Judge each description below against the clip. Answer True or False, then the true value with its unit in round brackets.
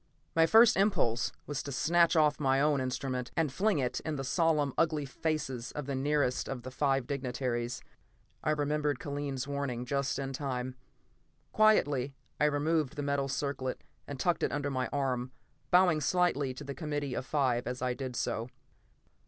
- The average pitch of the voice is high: False (140 Hz)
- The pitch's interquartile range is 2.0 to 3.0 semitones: True (2.6 semitones)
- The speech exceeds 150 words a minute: True (170 wpm)